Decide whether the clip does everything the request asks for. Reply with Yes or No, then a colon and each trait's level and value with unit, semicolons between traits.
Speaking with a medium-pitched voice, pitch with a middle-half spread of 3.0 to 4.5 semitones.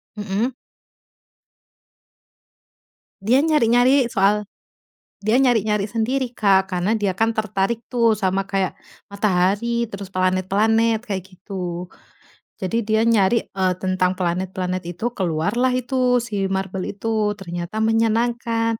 No: high, 210 Hz; average, 3.5 semitones